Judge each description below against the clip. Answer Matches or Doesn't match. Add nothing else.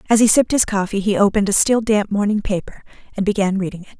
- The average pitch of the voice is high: Matches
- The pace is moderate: Doesn't match